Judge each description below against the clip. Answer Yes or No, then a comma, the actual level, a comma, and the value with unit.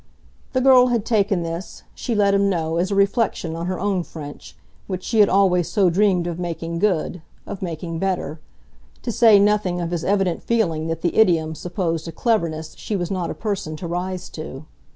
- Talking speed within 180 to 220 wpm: Yes, average, 195 wpm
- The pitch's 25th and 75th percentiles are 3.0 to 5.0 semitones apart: Yes, average, 3.3 semitones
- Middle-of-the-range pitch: Yes, medium, 180 Hz